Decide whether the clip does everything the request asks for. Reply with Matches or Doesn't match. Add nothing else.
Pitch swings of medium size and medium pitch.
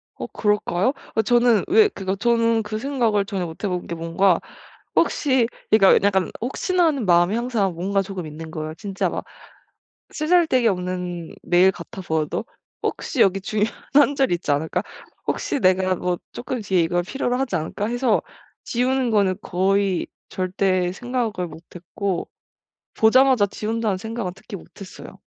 Doesn't match